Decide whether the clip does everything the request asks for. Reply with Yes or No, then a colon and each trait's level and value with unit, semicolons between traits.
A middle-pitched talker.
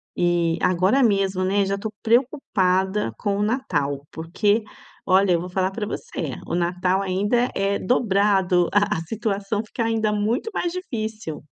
No: high, 195 Hz